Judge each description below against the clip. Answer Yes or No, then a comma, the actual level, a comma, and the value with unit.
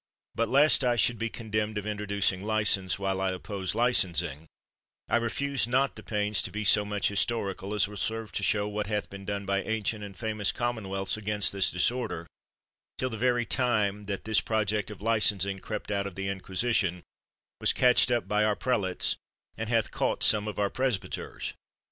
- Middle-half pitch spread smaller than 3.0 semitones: Yes, narrow, 2.5 semitones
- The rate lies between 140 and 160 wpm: No, average, 185 wpm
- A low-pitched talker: Yes, low, 105 Hz